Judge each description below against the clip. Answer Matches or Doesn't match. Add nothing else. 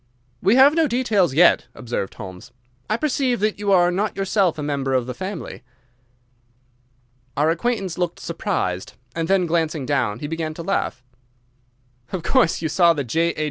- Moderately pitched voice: Matches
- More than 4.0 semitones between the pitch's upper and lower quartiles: Matches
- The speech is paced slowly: Doesn't match